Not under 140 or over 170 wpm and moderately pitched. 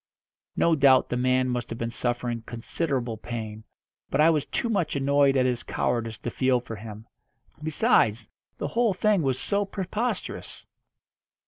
No: average, 155 wpm; low, 130 Hz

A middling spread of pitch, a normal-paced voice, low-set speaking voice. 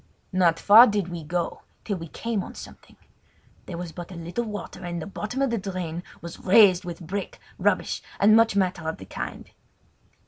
No: average, 3.3 semitones; average, 185 wpm; medium, 185 Hz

